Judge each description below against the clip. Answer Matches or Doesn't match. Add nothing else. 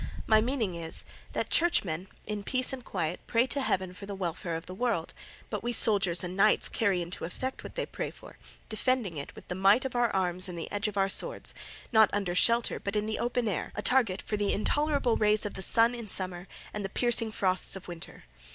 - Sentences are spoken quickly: Matches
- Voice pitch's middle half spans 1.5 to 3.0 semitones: Doesn't match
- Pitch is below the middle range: Doesn't match